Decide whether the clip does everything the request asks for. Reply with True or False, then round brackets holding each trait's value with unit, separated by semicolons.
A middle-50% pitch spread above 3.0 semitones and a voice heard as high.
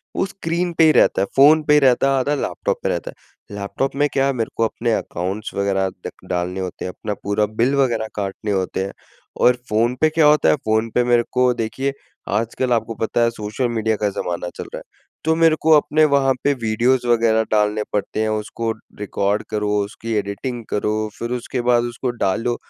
False (4.1 semitones; 115 Hz)